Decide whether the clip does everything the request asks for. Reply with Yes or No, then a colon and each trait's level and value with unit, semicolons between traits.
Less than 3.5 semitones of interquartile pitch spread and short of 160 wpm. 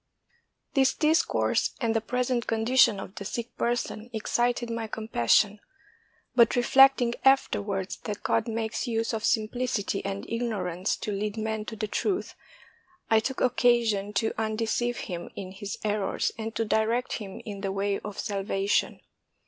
Yes: average, 2.8 semitones; average, 150 wpm